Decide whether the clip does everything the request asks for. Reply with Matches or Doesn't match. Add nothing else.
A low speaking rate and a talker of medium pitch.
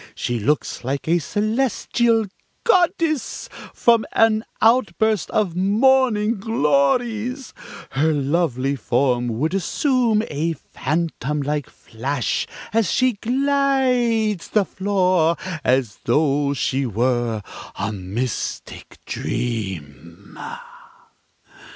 Matches